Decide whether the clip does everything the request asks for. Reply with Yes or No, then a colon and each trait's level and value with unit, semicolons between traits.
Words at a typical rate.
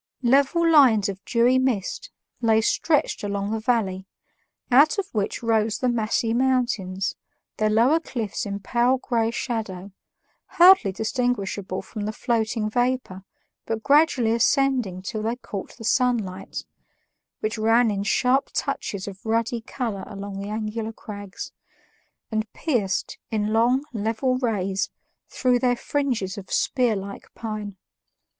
No: slow, 130 wpm